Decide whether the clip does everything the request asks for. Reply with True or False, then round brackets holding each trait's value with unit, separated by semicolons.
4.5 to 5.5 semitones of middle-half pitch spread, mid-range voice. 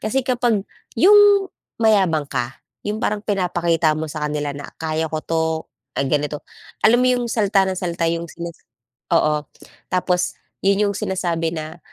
True (4.8 semitones; 170 Hz)